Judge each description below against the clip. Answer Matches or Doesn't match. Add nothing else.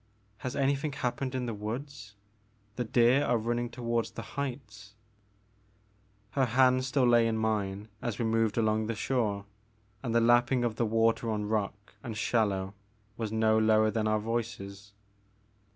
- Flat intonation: Matches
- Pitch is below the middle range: Matches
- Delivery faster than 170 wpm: Doesn't match